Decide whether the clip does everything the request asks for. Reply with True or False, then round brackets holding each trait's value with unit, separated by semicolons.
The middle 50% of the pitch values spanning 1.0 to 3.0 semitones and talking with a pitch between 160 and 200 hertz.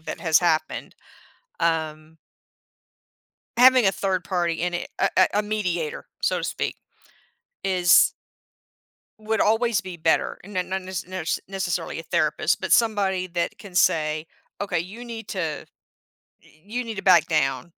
False (3.7 semitones; 185 Hz)